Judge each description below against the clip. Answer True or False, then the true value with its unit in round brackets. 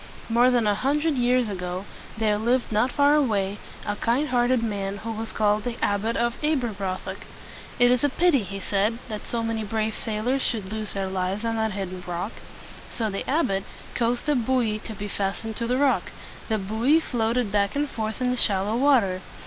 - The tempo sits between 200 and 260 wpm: True (205 wpm)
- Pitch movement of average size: True (3.5 semitones)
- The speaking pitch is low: False (225 Hz)